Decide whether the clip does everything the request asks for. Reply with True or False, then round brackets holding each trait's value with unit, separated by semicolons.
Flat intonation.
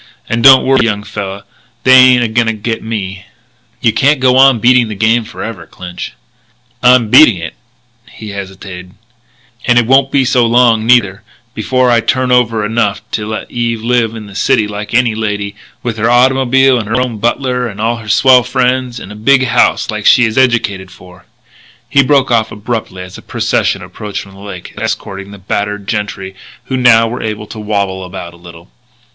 False (3.4 semitones)